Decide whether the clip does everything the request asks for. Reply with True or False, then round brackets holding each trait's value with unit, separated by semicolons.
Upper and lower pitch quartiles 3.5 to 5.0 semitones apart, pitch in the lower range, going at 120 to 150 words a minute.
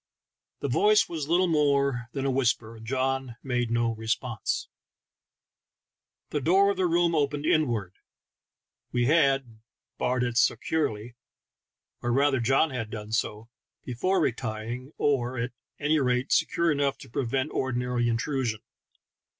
True (3.8 semitones; 130 Hz; 140 wpm)